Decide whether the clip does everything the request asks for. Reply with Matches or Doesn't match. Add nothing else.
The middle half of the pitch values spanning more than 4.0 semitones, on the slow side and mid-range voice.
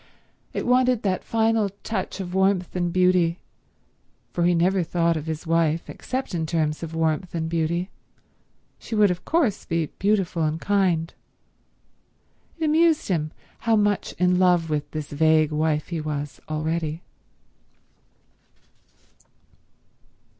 Doesn't match